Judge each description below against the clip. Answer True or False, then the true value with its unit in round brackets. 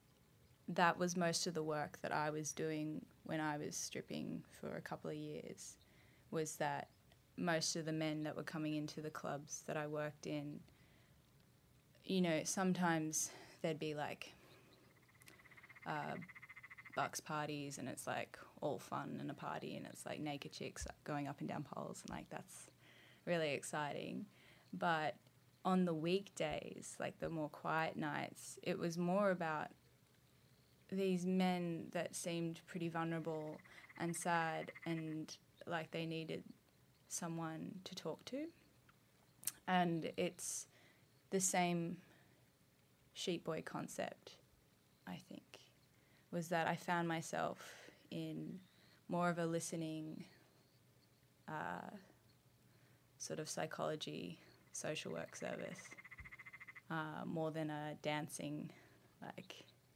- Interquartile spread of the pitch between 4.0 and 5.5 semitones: False (2.4 semitones)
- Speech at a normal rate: False (130 wpm)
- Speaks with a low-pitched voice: False (160 Hz)